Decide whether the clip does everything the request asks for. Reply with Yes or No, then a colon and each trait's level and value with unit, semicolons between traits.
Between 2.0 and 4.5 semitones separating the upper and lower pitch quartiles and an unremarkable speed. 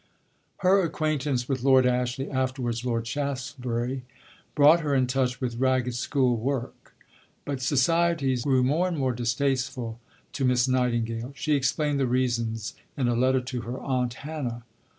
Yes: narrow, 2.4 semitones; average, 150 wpm